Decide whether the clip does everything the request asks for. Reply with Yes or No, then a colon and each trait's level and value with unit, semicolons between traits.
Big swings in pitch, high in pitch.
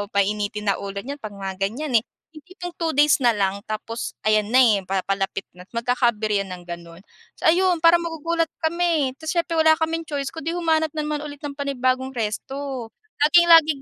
Yes: wide, 7.2 semitones; very high, 270 Hz